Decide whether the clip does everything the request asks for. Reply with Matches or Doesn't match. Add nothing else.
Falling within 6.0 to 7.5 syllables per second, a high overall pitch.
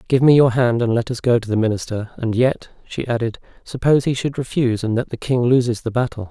Doesn't match